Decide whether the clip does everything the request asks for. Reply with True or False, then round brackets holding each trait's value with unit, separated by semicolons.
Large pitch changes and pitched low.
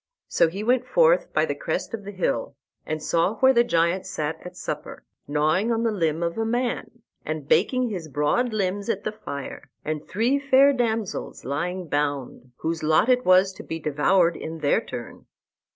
False (6.6 semitones; 185 Hz)